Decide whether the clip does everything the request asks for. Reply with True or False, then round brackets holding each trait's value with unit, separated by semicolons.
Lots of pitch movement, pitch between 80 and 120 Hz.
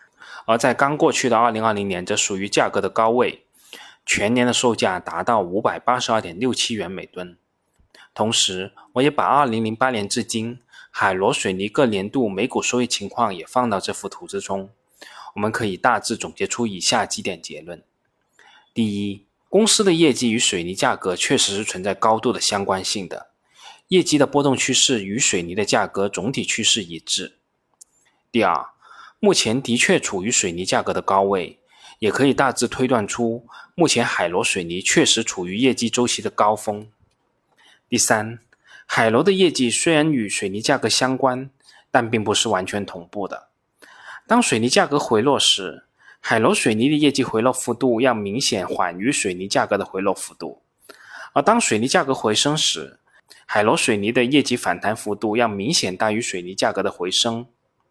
False (4.0 semitones; 115 Hz)